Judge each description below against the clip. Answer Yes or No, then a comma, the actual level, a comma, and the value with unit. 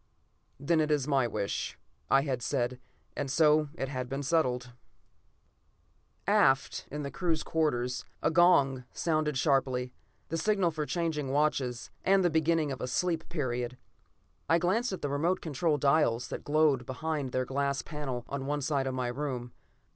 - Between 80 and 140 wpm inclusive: No, average, 160 wpm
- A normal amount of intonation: Yes, average, 3.7 semitones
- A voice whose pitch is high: No, medium, 145 Hz